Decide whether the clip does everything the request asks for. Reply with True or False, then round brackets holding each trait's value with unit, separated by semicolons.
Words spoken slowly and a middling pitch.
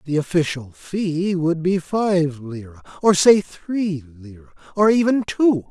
True (125 wpm; 170 Hz)